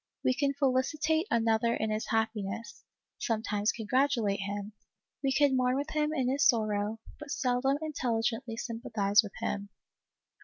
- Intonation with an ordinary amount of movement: Yes, average, 4.2 semitones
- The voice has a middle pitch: No, high, 235 Hz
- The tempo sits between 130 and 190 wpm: Yes, average, 145 wpm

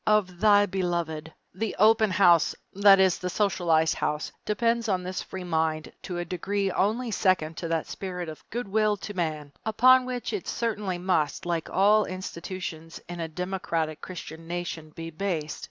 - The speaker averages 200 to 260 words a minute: No, average, 170 wpm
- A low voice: No, medium, 185 Hz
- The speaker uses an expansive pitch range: No, average, 3.8 semitones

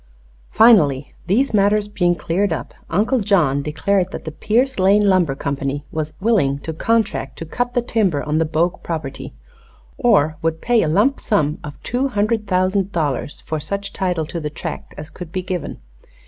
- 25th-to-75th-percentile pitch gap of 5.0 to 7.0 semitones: Yes, wide, 5.4 semitones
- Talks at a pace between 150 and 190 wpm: Yes, average, 175 wpm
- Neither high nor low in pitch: Yes, medium, 180 Hz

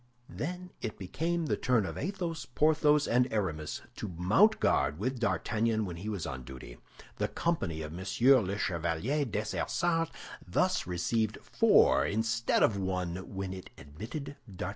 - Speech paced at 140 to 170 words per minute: Yes, average, 150 wpm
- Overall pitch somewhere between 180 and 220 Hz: No, low, 110 Hz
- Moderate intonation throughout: No, wide, 8.0 semitones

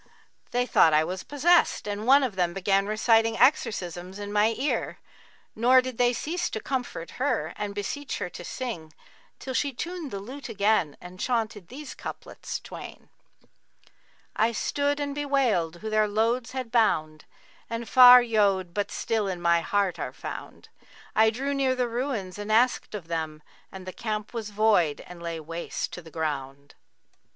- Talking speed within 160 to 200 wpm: Yes, average, 170 wpm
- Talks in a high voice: Yes, high, 215 Hz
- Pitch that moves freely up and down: Yes, wide, 5.8 semitones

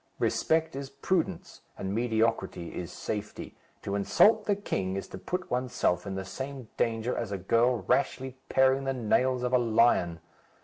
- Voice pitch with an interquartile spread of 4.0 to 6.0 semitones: Yes, average, 5.1 semitones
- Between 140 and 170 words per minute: Yes, average, 165 wpm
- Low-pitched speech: Yes, low, 120 Hz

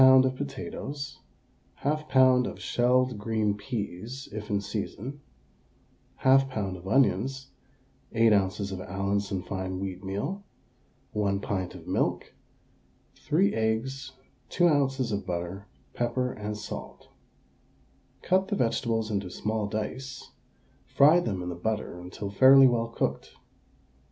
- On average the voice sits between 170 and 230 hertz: No, low, 110 Hz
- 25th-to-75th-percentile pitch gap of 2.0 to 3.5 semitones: No, average, 5.0 semitones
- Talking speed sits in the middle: No, slow, 120 wpm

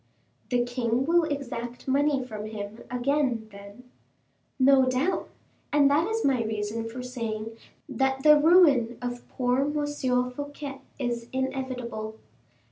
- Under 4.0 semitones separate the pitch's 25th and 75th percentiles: Yes, average, 3.2 semitones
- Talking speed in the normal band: No, slow, 125 wpm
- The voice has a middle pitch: No, very high, 255 Hz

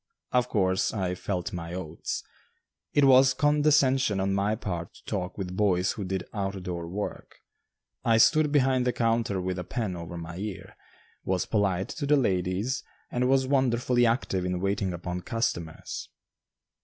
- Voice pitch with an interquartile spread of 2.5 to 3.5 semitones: No, wide, 5.5 semitones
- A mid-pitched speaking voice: No, low, 100 Hz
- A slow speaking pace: No, average, 160 wpm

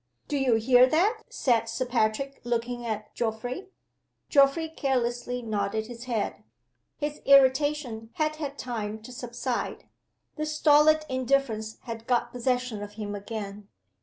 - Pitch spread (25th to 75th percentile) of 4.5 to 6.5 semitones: No, average, 3.7 semitones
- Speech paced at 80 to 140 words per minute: Yes, slow, 135 wpm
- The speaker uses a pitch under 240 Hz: No, high, 245 Hz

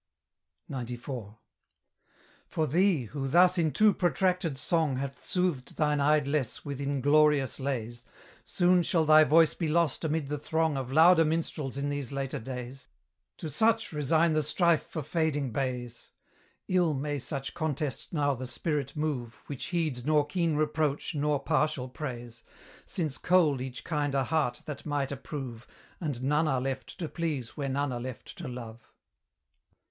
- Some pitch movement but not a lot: Yes, average, 3.3 semitones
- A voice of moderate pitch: Yes, medium, 145 Hz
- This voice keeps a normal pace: Yes, average, 150 wpm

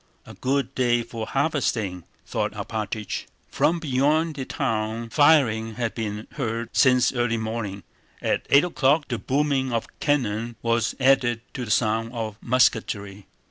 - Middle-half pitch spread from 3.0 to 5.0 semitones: Yes, average, 3.5 semitones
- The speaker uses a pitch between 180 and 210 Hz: No, low, 120 Hz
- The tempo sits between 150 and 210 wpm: No, average, 140 wpm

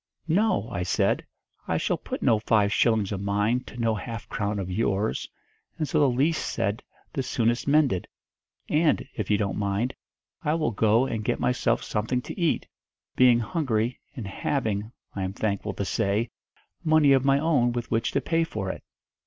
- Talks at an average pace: Yes, average, 180 wpm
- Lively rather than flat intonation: No, average, 4.9 semitones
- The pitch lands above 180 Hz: No, low, 115 Hz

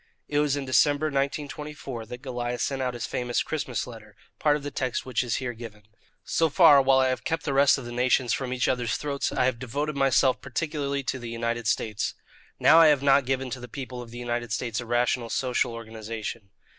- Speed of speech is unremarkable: No, fast, 220 wpm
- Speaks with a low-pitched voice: Yes, low, 130 Hz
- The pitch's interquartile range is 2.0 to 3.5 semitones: Yes, average, 2.8 semitones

